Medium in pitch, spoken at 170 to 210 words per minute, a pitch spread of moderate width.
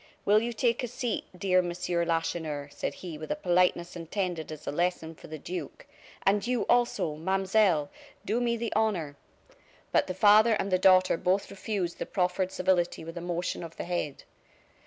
Yes: medium, 180 Hz; average, 185 wpm; average, 3.4 semitones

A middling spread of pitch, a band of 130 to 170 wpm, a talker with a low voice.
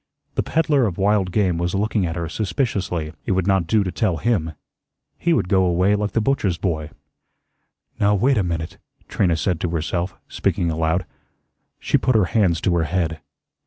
No: average, 3.6 semitones; average, 185 wpm; very low, 95 Hz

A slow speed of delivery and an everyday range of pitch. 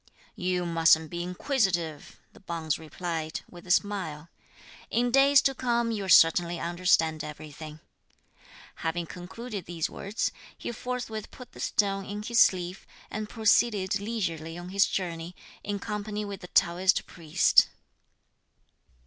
Yes: slow, 130 wpm; average, 4.2 semitones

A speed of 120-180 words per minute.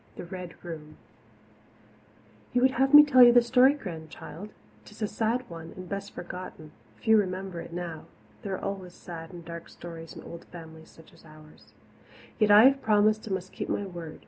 No: average, 190 wpm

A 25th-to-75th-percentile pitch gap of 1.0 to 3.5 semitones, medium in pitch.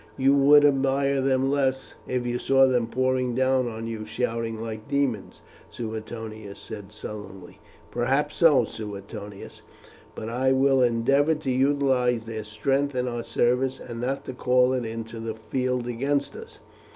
No: average, 3.0 semitones; low, 125 Hz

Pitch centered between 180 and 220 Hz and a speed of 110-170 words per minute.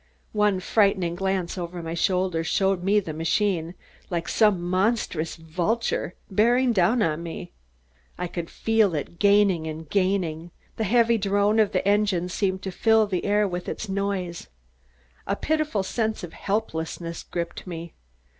Yes: high, 190 Hz; average, 145 wpm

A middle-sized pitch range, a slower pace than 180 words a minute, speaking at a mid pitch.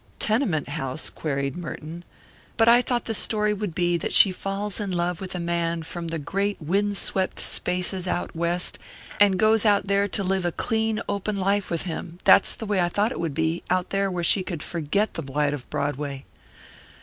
No: average, 3.6 semitones; average, 200 wpm; medium, 180 Hz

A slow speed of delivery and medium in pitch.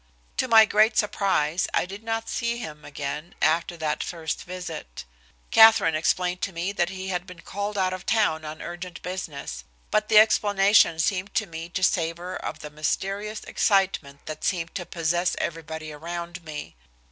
No: average, 170 wpm; medium, 180 Hz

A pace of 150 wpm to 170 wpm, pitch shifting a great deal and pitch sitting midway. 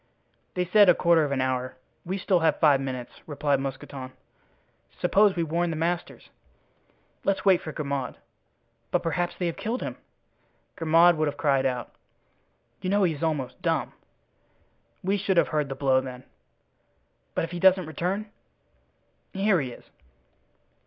No: average, 160 wpm; average, 4.7 semitones; medium, 160 Hz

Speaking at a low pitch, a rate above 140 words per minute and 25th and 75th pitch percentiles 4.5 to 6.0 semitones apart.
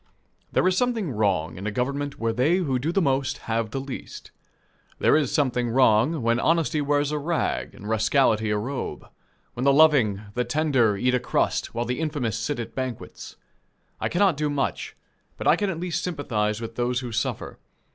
Yes: low, 130 Hz; average, 190 wpm; average, 4.8 semitones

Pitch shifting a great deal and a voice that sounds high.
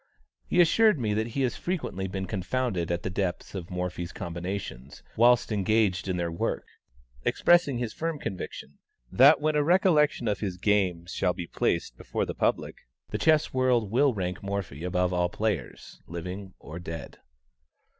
No: wide, 6.1 semitones; low, 100 Hz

